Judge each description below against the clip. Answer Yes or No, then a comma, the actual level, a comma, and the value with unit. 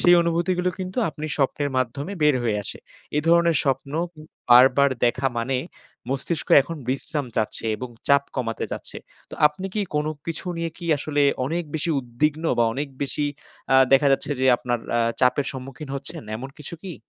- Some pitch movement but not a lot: Yes, average, 4.1 semitones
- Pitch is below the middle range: No, medium, 145 Hz